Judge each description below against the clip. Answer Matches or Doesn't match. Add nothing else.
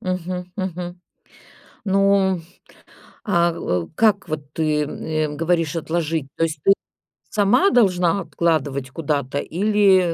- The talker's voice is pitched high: Doesn't match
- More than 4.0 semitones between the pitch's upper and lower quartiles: Doesn't match